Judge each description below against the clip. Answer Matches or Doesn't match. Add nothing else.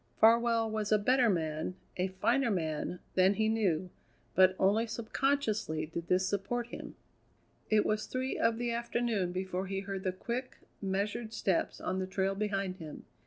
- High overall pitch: Matches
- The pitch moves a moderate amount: Matches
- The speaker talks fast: Doesn't match